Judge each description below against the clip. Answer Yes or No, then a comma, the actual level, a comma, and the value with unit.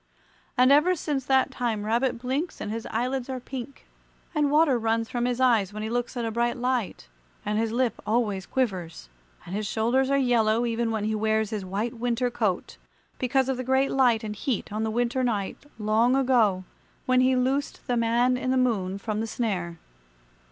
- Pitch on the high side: Yes, high, 235 Hz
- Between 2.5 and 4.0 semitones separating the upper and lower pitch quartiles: Yes, average, 2.9 semitones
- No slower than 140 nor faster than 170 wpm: No, average, 195 wpm